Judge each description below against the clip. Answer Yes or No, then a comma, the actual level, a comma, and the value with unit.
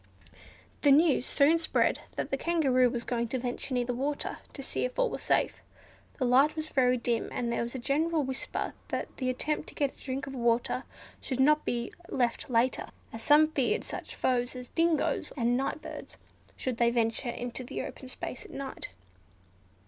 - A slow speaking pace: No, average, 195 wpm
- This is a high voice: Yes, very high, 255 Hz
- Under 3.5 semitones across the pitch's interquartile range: Yes, average, 2.8 semitones